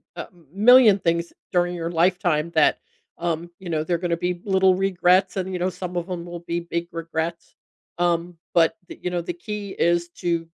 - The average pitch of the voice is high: No, medium, 175 Hz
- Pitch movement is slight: Yes, narrow, 1.4 semitones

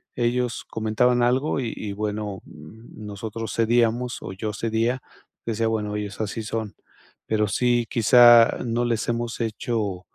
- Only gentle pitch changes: Yes, narrow, 2.0 semitones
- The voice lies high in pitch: No, low, 115 Hz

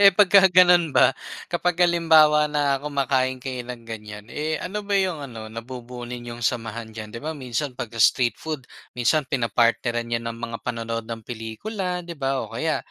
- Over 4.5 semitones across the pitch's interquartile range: Yes, average, 5.3 semitones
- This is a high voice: No, low, 130 Hz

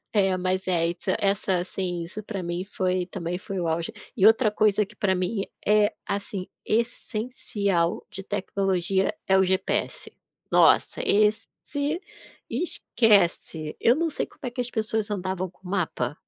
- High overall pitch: Yes, high, 195 Hz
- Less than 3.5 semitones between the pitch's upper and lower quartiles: Yes, average, 2.8 semitones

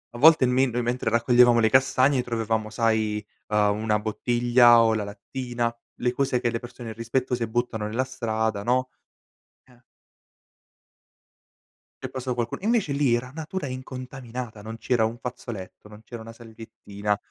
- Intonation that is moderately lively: No, narrow, 2.3 semitones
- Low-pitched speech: Yes, low, 120 Hz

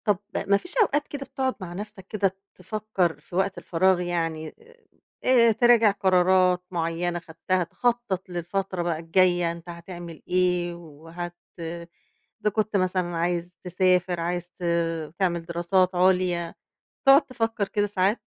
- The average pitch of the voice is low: No, medium, 180 Hz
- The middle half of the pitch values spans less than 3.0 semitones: Yes, narrow, 2.5 semitones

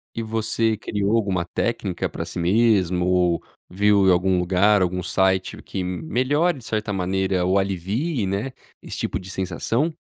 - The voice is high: No, very low, 95 Hz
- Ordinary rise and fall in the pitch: Yes, average, 3.5 semitones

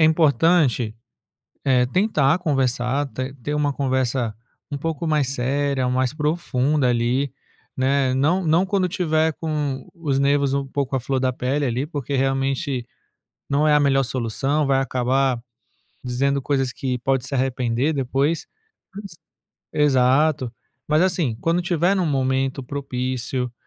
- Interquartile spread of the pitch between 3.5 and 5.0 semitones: No, narrow, 2.6 semitones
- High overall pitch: No, low, 135 Hz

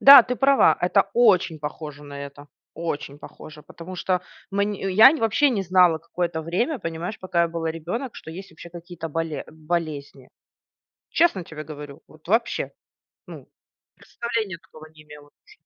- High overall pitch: No, medium, 170 Hz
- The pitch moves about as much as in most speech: Yes, average, 4.3 semitones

